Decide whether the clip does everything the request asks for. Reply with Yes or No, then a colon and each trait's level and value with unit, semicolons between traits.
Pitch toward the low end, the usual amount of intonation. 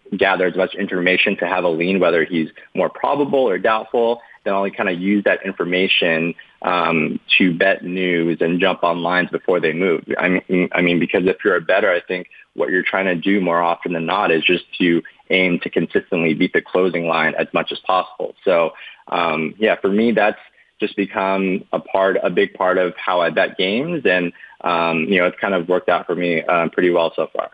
No: very low, 90 Hz; narrow, 2.2 semitones